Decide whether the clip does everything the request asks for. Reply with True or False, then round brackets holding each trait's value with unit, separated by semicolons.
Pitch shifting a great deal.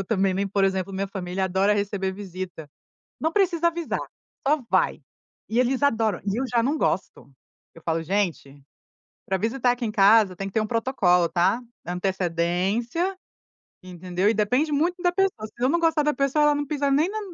True (7.2 semitones)